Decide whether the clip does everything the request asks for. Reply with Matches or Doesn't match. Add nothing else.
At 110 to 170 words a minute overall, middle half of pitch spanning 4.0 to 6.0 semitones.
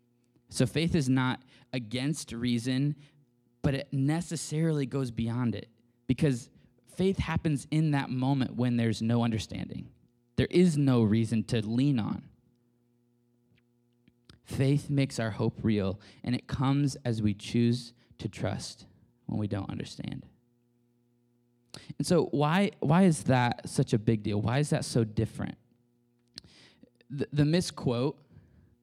Doesn't match